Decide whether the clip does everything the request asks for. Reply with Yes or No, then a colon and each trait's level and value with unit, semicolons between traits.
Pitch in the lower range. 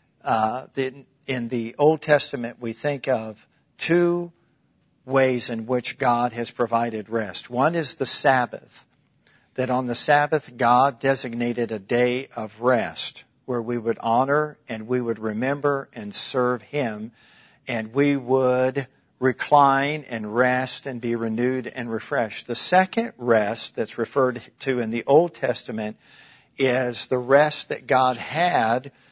Yes: low, 125 Hz